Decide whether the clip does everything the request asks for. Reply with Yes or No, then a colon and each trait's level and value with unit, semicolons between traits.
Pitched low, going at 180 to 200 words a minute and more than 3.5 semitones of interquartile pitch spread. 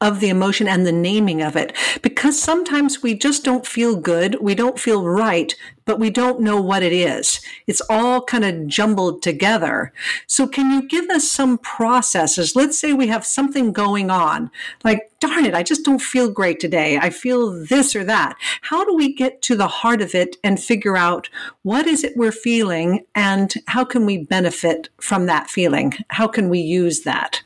No: high, 220 Hz; average, 195 wpm; wide, 5.5 semitones